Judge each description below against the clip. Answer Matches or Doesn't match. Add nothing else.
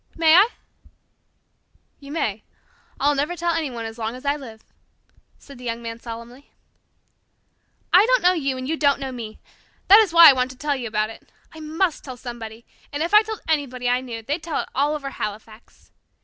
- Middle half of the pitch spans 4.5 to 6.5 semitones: Matches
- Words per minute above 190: Matches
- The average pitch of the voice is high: Matches